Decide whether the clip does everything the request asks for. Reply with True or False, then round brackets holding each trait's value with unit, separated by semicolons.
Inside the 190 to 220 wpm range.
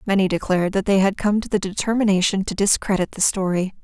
True (205 wpm)